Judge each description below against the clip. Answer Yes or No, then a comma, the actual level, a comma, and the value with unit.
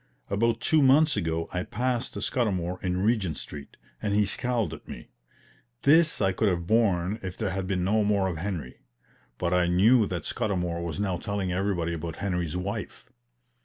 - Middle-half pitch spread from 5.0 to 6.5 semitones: No, average, 3.8 semitones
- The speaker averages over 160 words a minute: Yes, average, 175 wpm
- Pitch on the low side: Yes, very low, 95 Hz